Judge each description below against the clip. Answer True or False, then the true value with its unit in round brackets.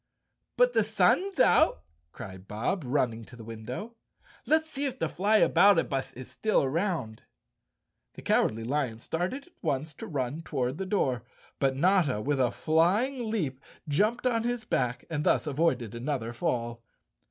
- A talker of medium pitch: True (150 Hz)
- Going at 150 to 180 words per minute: True (155 wpm)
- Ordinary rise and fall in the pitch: False (8.8 semitones)